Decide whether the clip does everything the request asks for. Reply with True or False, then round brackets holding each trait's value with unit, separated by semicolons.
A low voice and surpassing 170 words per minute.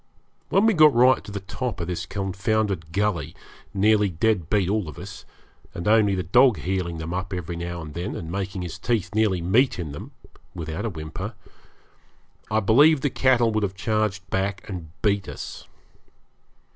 True (100 Hz; 185 wpm)